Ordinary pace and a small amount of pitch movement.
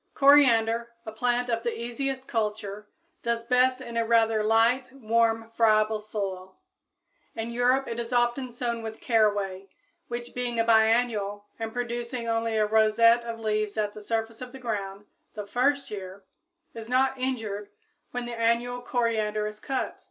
Yes: average, 160 wpm; narrow, 2.2 semitones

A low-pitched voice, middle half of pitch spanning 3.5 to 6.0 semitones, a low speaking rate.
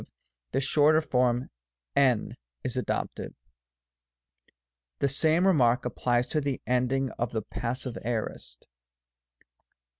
No: low, 125 Hz; narrow, 2.5 semitones; slow, 110 wpm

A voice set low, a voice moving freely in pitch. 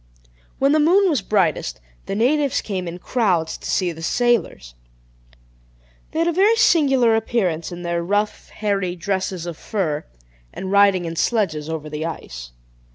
No: high, 195 Hz; wide, 6.4 semitones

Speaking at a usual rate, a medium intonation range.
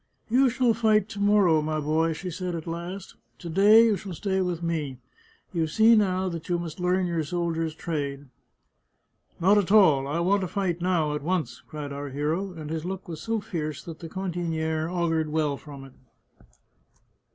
Yes: average, 195 wpm; average, 3.4 semitones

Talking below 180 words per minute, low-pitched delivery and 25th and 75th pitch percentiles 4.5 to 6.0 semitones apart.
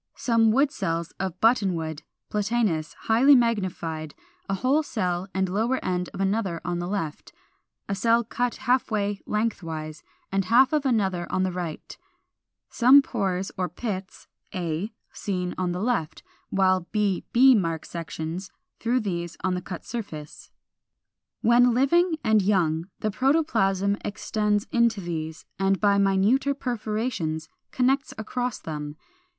No: average, 140 wpm; high, 195 Hz; average, 5.0 semitones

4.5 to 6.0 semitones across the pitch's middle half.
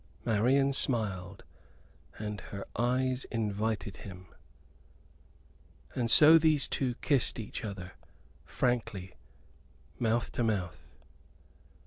No: average, 4.1 semitones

